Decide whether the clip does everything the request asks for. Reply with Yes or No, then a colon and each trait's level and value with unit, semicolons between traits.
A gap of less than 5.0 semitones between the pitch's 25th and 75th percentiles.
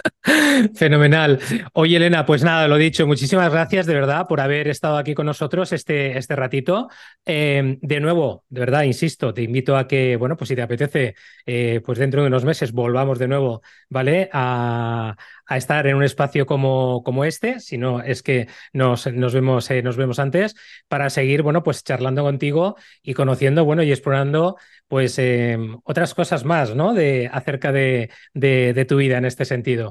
Yes: average, 3.4 semitones